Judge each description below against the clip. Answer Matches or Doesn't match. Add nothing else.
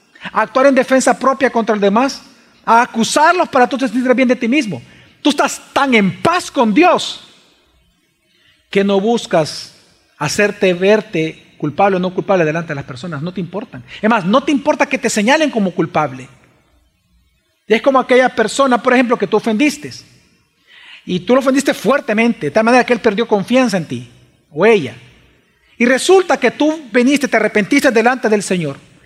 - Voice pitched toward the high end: Matches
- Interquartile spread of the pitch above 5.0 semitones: Matches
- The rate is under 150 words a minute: Doesn't match